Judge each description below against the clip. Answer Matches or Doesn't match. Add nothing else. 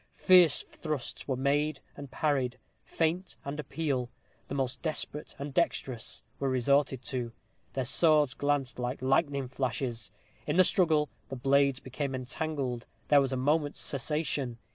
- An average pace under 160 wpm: Matches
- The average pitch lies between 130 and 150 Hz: Matches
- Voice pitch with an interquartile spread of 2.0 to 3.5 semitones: Matches